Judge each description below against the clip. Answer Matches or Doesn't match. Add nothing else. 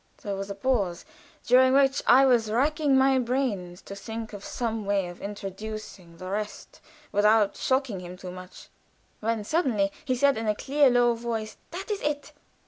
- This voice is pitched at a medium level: Doesn't match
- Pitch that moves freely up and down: Doesn't match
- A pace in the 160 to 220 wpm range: Matches